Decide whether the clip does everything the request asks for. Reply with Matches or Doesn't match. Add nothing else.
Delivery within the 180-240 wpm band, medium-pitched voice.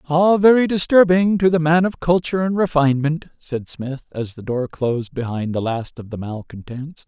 Matches